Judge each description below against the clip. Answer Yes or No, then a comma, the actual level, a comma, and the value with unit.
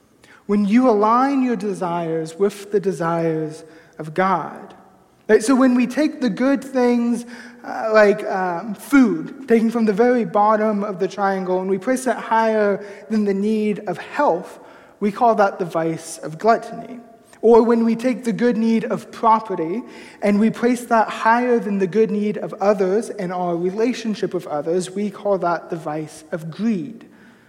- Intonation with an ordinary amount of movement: Yes, average, 3.5 semitones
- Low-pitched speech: No, high, 215 Hz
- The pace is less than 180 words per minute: Yes, average, 170 wpm